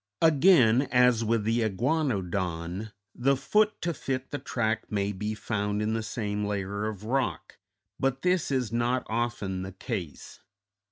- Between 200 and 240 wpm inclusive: No, average, 150 wpm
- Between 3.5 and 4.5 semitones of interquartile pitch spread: Yes, average, 4.0 semitones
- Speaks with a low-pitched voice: Yes, low, 110 Hz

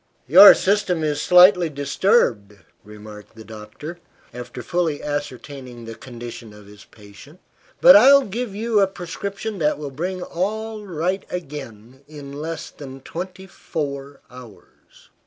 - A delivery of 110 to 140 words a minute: Yes, slow, 135 wpm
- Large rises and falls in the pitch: Yes, wide, 7.2 semitones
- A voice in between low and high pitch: Yes, medium, 150 Hz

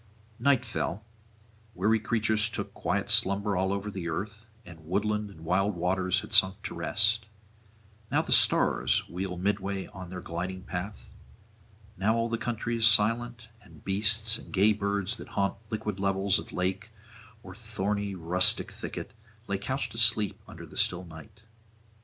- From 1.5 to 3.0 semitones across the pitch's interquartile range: Yes, average, 2.7 semitones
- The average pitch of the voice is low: Yes, low, 100 Hz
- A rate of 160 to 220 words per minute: No, average, 150 wpm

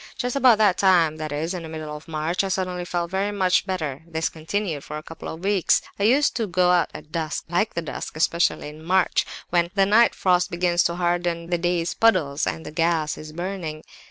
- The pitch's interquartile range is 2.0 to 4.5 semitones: Yes, average, 2.9 semitones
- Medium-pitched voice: Yes, medium, 175 Hz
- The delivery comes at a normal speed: No, fast, 220 wpm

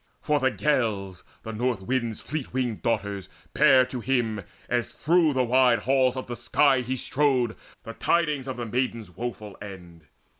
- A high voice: No, low, 125 Hz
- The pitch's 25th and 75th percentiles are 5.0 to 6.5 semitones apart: No, average, 3.2 semitones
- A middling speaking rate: Yes, average, 165 wpm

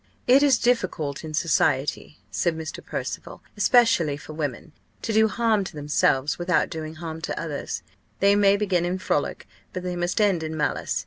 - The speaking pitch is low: No, medium, 175 Hz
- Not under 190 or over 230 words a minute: No, average, 175 wpm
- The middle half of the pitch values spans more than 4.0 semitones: Yes, average, 4.6 semitones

